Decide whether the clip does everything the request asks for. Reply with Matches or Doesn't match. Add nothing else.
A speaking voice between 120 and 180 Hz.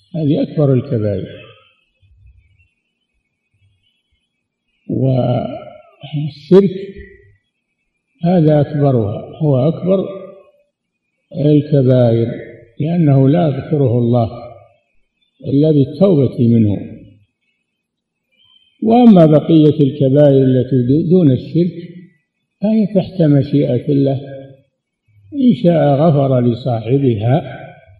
Matches